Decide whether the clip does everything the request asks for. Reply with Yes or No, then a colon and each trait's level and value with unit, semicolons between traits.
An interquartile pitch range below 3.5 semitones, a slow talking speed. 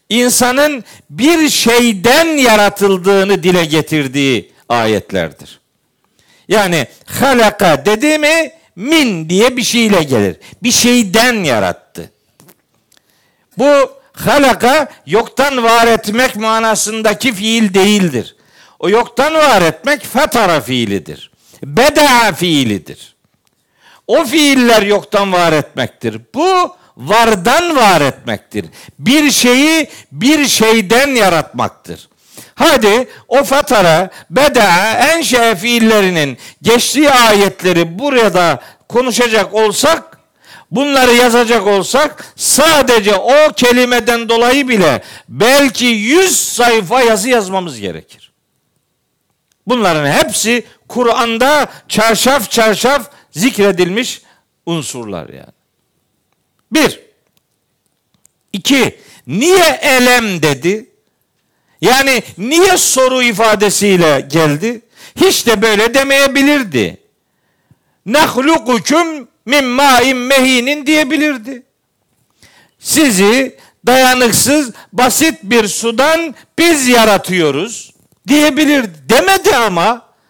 No: wide, 5.4 semitones; slow, 80 wpm